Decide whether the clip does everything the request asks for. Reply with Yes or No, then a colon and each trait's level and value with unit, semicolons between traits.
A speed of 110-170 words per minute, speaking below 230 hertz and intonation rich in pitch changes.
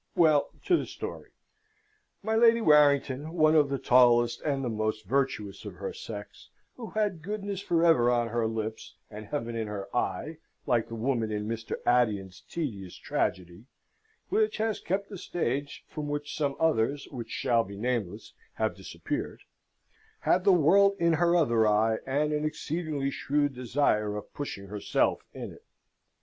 Yes: average, 160 wpm; low, 135 Hz; wide, 6.3 semitones